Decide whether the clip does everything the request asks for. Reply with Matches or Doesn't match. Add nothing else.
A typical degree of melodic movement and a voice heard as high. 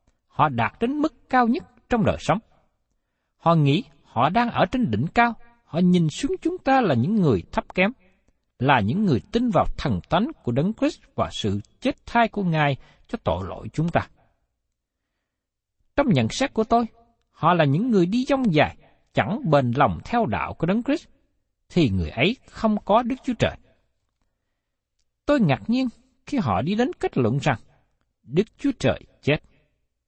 Doesn't match